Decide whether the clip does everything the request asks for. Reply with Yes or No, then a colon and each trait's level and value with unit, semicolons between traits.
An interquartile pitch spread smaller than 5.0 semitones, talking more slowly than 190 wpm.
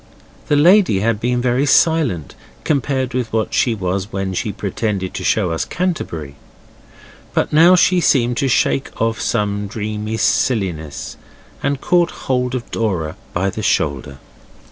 No: wide, 5.6 semitones; average, 145 wpm